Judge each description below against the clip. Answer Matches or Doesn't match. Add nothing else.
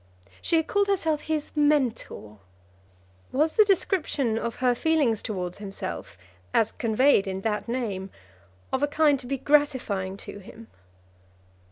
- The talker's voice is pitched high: Matches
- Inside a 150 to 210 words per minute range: Doesn't match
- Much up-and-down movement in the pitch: Matches